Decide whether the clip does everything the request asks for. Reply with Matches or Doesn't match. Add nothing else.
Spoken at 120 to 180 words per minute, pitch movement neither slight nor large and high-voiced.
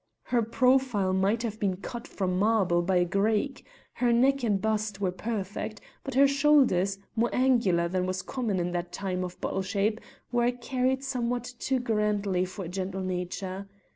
Matches